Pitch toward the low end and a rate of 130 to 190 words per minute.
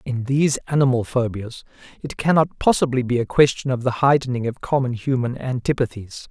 Yes: low, 130 Hz; average, 160 wpm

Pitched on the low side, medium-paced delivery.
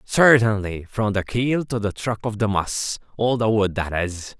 Yes: low, 110 Hz; average, 190 wpm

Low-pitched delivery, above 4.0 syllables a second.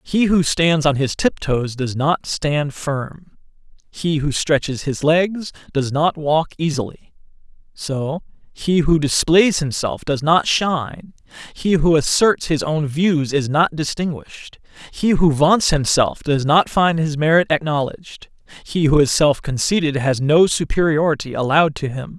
No: medium, 155 Hz; 4.3 syllables/s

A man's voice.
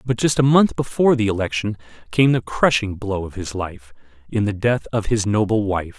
Yes: male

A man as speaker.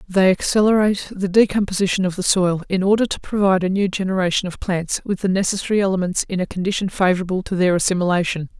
No: female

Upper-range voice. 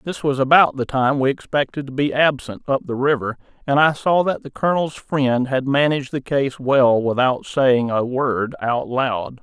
No: low, 135 Hz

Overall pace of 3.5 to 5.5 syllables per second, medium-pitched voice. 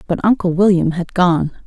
Yes: 5.0 syllables/s; medium, 180 Hz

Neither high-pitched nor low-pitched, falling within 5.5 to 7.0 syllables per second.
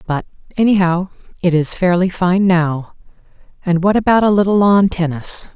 No: medium, 180 Hz; 4.9 syllables/s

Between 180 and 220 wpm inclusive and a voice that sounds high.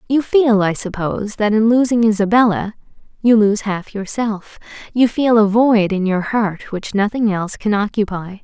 No: average, 170 wpm; high, 210 Hz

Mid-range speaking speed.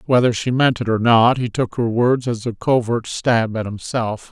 No: fast, 225 wpm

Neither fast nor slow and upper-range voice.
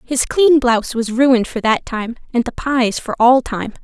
No: fast, 220 wpm; high, 245 Hz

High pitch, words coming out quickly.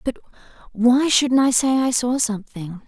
No: high, 245 Hz; average, 165 wpm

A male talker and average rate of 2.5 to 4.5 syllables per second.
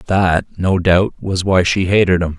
Yes: male; 4.4 syllables/s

